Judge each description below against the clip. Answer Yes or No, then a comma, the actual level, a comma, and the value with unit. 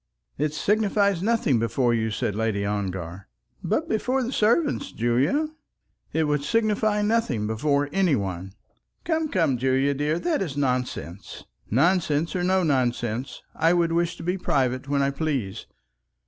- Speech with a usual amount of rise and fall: No, wide, 8.1 semitones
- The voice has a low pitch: No, medium, 145 Hz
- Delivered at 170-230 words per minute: No, average, 145 wpm